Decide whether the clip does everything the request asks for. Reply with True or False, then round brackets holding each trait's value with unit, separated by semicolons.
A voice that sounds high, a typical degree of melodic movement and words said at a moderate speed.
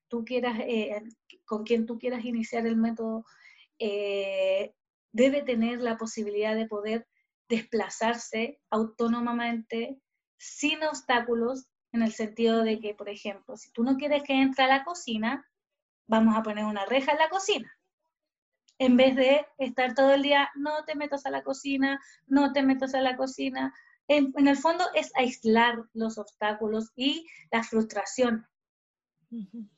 True (240 Hz; 3.9 semitones; 150 wpm)